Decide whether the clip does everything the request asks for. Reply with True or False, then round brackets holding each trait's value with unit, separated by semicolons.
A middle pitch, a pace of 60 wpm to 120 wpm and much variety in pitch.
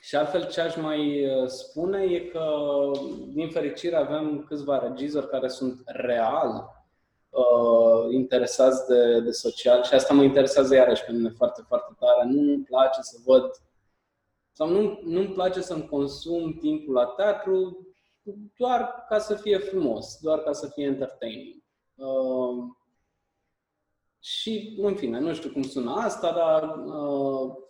False (150 Hz; 140 wpm; 6.8 semitones)